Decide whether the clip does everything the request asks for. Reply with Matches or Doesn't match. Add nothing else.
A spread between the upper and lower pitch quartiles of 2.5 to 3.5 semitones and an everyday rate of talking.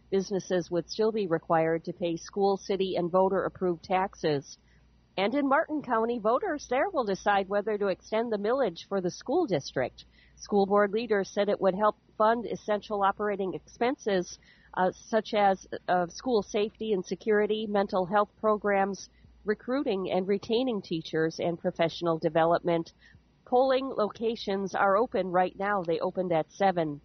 Matches